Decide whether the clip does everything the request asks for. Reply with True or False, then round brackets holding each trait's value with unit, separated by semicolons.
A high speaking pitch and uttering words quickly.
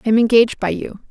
True (220 Hz; 270 wpm)